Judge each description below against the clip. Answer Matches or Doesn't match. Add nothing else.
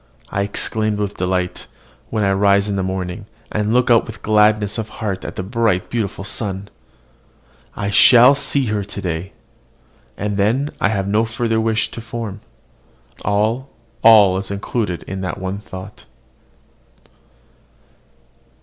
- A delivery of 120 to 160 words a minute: Matches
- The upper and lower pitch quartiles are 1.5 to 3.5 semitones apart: Matches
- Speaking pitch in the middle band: Doesn't match